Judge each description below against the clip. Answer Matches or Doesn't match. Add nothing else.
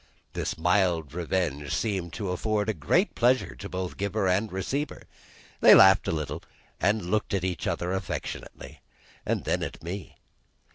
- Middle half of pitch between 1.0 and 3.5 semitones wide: Matches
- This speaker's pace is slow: Doesn't match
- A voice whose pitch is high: Doesn't match